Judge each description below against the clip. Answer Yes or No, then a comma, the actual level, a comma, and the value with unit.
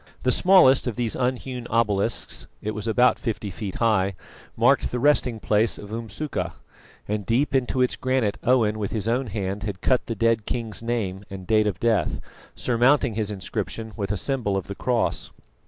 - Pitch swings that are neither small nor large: Yes, average, 3.1 semitones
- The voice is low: Yes, low, 115 Hz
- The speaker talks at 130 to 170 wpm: No, average, 180 wpm